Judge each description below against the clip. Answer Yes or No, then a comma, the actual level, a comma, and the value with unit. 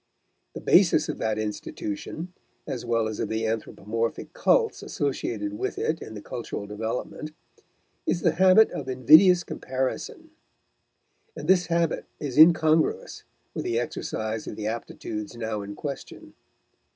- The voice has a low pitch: Yes, low, 120 Hz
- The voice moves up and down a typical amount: No, wide, 6.4 semitones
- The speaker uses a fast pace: No, average, 140 wpm